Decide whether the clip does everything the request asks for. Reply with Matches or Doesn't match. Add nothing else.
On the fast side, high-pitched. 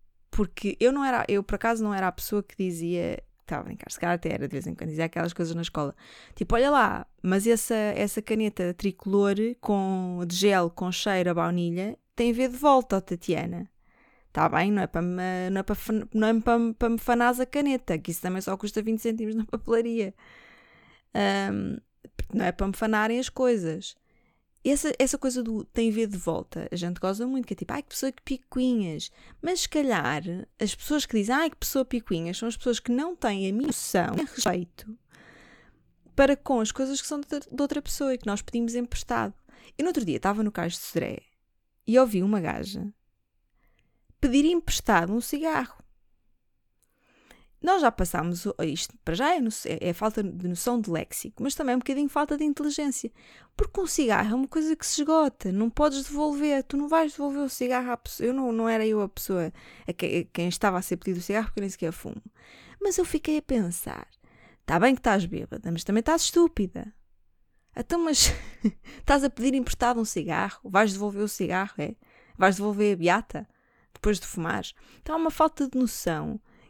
Matches